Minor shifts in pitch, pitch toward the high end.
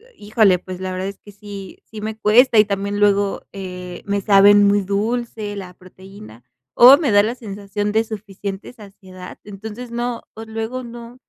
Yes: narrow, 2.2 semitones; high, 205 Hz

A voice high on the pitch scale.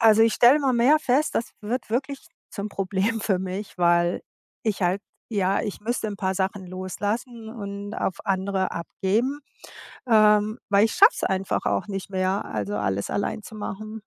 Yes: high, 205 Hz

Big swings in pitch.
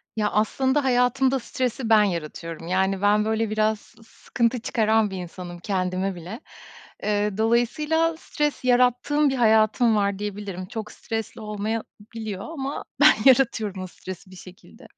No: average, 4.0 semitones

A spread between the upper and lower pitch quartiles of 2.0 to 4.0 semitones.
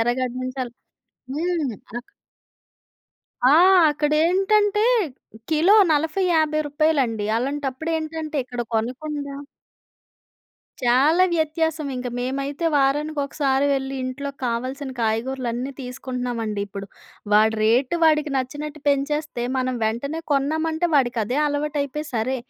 Yes: average, 3.6 semitones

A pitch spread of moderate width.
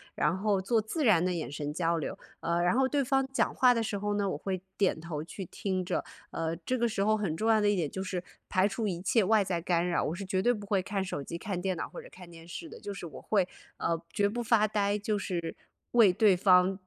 Yes: average, 3.6 semitones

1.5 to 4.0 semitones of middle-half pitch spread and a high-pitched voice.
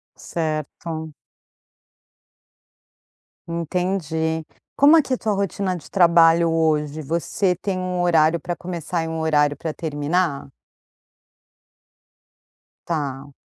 No: narrow, 2.6 semitones; medium, 165 Hz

